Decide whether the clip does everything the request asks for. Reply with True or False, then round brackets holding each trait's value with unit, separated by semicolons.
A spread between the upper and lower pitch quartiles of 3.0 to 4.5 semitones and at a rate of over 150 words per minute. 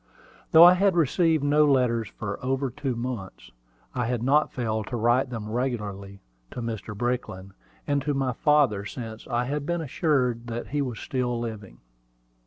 True (3.9 semitones; 170 wpm)